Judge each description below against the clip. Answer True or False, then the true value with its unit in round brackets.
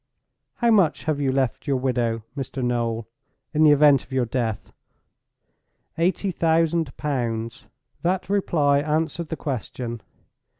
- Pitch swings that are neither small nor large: True (4.8 semitones)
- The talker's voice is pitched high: False (140 Hz)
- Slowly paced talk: True (130 wpm)